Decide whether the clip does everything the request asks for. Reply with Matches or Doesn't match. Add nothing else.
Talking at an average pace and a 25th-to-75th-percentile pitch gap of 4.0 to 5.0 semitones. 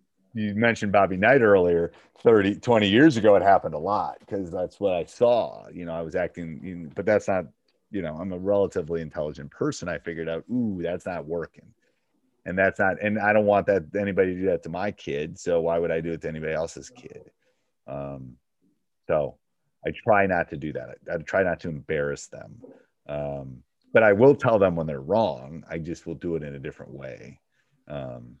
Doesn't match